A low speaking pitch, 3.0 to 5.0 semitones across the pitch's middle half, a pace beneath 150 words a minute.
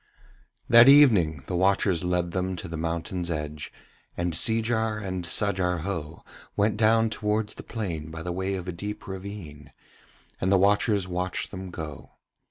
No: very low, 95 Hz; average, 3.6 semitones; average, 160 wpm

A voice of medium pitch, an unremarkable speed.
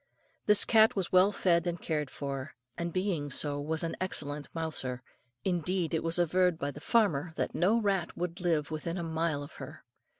Yes: medium, 165 Hz; average, 190 wpm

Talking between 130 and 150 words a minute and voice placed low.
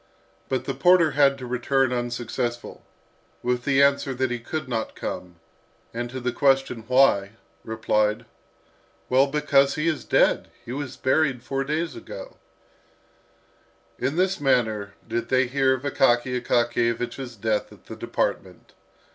Yes: average, 140 wpm; low, 130 Hz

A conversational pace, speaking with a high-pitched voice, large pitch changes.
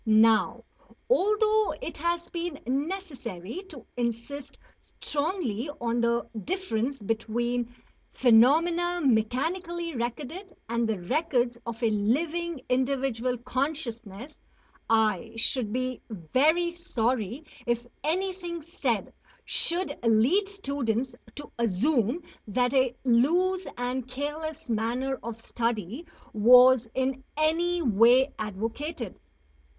No: slow, 100 wpm; very high, 255 Hz; wide, 5.9 semitones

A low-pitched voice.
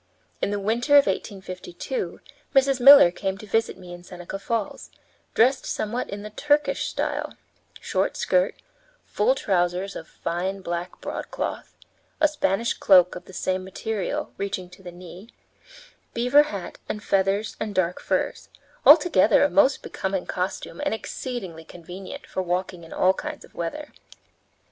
No: high, 195 Hz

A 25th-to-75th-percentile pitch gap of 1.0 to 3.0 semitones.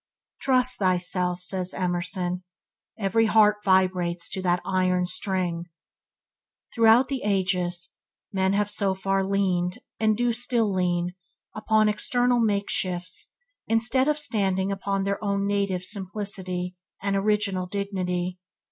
Yes: narrow, 2.6 semitones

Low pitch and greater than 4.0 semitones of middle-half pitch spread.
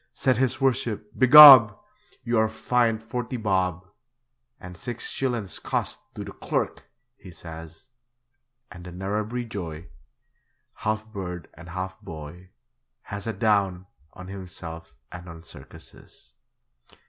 Yes: low, 100 Hz; average, 4.4 semitones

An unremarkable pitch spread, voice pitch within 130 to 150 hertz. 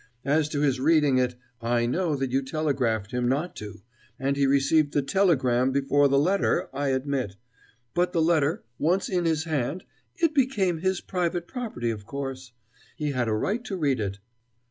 Yes: average, 4.9 semitones; medium, 140 Hz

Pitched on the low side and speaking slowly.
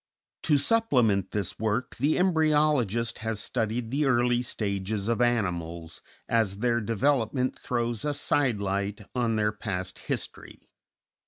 Yes: low, 115 Hz; slow, 130 wpm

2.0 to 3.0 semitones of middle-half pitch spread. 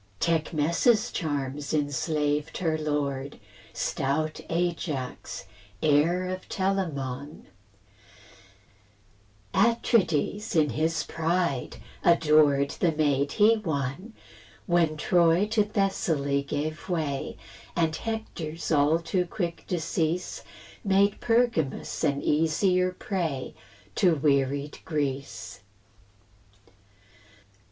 No: average, 4.0 semitones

